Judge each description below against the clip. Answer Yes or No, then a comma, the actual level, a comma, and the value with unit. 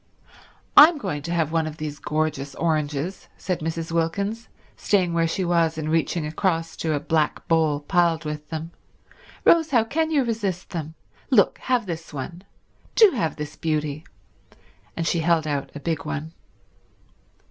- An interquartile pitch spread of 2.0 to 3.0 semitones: Yes, average, 2.7 semitones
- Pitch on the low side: No, medium, 165 Hz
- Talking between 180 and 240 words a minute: No, average, 160 wpm